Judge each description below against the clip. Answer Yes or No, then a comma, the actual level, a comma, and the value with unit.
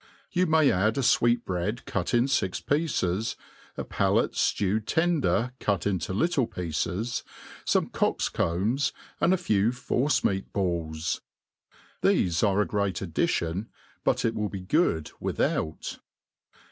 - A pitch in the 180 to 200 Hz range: No, low, 105 Hz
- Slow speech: Yes, slow, 130 wpm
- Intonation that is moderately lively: No, wide, 5.7 semitones